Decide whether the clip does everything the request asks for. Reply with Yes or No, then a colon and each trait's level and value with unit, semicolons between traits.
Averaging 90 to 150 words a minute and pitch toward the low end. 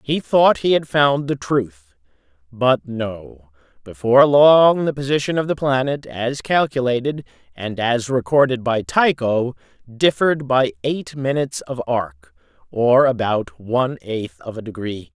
Yes: average, 140 wpm; low, 130 Hz